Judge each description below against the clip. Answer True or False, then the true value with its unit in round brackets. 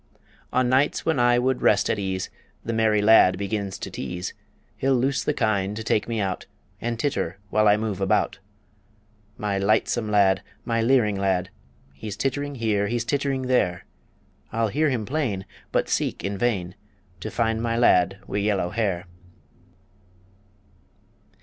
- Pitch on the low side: True (110 Hz)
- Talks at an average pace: True (155 wpm)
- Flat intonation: False (3.9 semitones)